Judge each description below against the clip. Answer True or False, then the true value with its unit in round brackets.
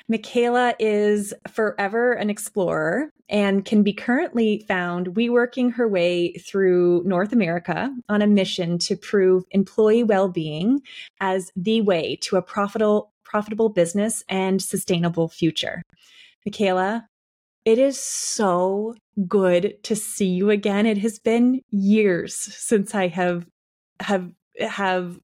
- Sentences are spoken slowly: True (125 wpm)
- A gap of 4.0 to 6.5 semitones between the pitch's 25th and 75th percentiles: False (3.2 semitones)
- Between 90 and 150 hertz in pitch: False (205 Hz)